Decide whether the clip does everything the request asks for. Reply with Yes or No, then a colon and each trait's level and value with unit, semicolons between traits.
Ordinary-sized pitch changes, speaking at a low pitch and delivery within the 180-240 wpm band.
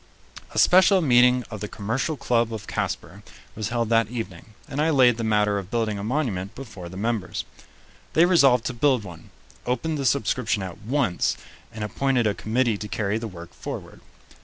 Yes: average, 3.7 semitones; low, 115 Hz; average, 185 wpm